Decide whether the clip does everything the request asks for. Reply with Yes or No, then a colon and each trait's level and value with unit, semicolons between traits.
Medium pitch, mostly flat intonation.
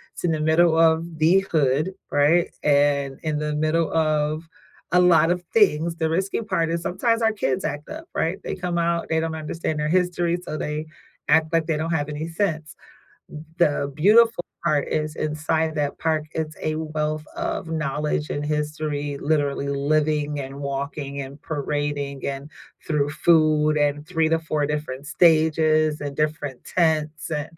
Yes: medium, 155 Hz; narrow, 1.8 semitones